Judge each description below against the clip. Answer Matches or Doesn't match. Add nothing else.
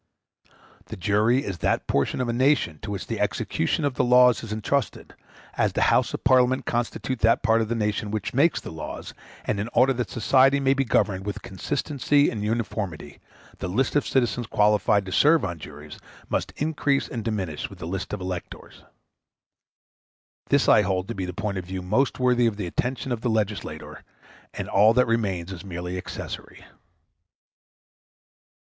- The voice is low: Matches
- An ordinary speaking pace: Matches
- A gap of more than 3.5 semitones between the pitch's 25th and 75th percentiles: Matches